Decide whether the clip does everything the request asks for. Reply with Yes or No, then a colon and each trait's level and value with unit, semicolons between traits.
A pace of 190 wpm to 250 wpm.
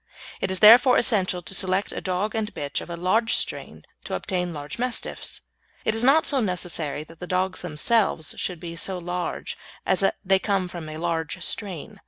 Yes: average, 195 wpm